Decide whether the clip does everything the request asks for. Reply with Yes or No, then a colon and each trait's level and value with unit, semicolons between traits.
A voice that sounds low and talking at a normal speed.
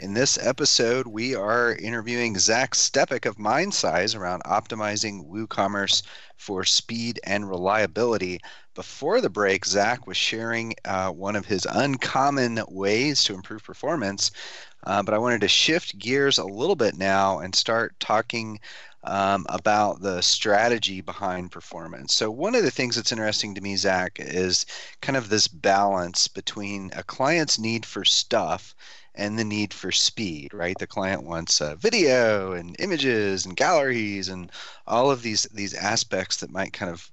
Yes: low, 105 Hz; average, 160 wpm